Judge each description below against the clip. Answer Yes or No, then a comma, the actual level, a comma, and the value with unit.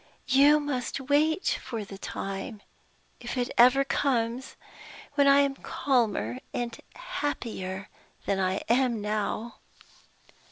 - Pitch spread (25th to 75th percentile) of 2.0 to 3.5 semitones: No, average, 4.8 semitones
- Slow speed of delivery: Yes, slow, 115 wpm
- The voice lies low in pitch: No, high, 245 Hz